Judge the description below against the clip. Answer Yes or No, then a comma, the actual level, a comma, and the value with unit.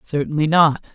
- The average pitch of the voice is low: No, medium, 150 Hz